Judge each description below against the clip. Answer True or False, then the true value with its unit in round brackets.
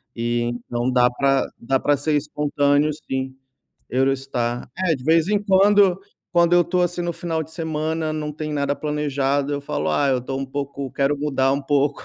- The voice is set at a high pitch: False (145 Hz)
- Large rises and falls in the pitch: False (3.1 semitones)